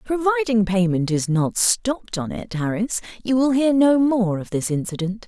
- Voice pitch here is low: No, high, 220 Hz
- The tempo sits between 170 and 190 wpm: Yes, average, 180 wpm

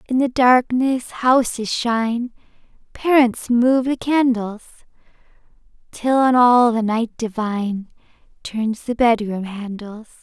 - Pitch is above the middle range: Yes, high, 235 Hz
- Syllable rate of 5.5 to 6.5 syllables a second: No, 3.8 syllables/s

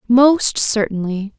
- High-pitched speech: Yes, high, 230 Hz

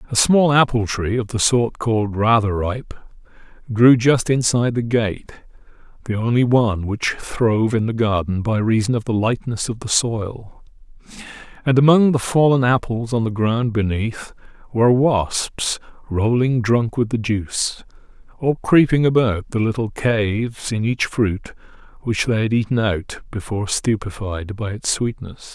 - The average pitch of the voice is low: Yes, low, 115 Hz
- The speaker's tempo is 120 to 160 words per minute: Yes, average, 155 wpm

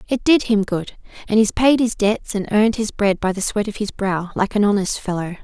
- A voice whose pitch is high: Yes, high, 210 Hz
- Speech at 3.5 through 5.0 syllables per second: No, 5.4 syllables/s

